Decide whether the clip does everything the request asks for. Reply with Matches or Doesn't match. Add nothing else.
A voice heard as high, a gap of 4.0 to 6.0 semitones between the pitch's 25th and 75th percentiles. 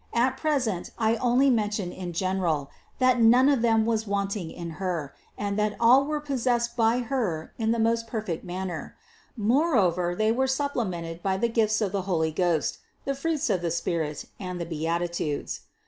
Matches